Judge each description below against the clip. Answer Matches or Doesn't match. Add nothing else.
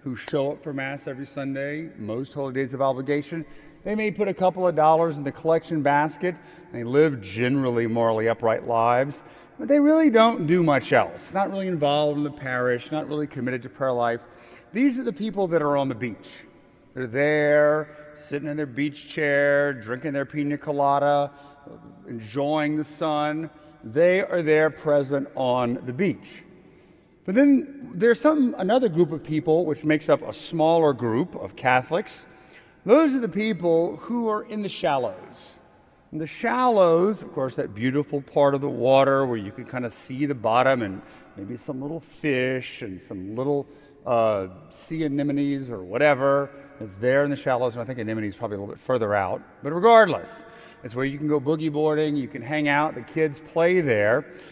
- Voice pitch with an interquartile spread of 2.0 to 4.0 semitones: Matches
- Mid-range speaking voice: Matches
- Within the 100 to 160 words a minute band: Doesn't match